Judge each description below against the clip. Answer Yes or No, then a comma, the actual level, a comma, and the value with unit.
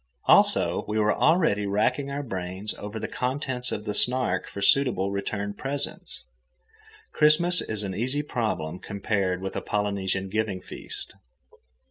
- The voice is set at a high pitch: No, low, 105 Hz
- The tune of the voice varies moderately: Yes, average, 4.8 semitones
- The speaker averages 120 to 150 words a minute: Yes, average, 140 wpm